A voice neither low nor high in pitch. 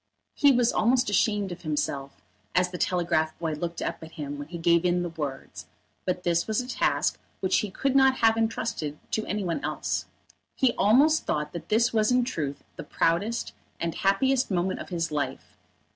Yes: medium, 180 Hz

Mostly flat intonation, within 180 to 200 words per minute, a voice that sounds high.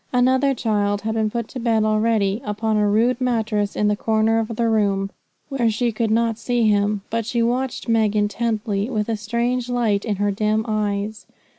Yes: narrow, 2.0 semitones; average, 190 wpm; high, 220 Hz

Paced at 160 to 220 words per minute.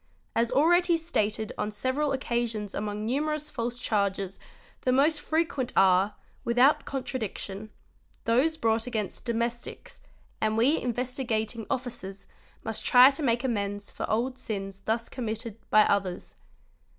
No: slow, 135 wpm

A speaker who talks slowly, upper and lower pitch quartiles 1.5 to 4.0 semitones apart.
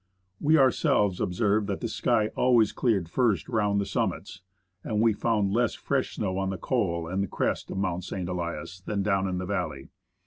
No: average, 185 wpm; average, 3.3 semitones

